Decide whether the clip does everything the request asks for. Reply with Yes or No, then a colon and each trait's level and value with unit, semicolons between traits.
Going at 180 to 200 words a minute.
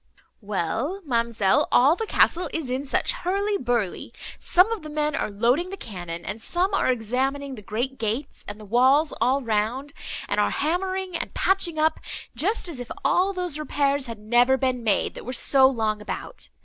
Yes: average, 185 wpm